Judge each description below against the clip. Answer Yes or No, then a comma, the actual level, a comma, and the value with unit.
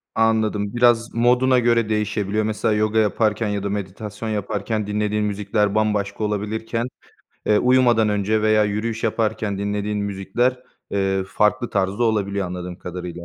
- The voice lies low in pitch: Yes, low, 105 Hz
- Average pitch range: No, narrow, 1.8 semitones